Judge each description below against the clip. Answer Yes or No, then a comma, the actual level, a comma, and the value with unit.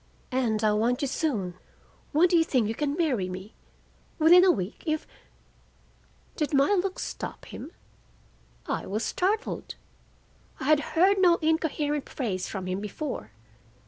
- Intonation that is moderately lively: No, wide, 7.3 semitones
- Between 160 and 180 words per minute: No, average, 145 wpm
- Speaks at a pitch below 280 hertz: No, very high, 285 Hz